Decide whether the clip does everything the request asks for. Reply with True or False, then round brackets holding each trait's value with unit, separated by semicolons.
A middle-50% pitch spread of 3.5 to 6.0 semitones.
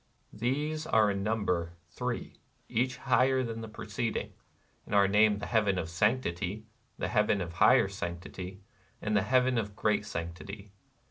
False (2.8 semitones)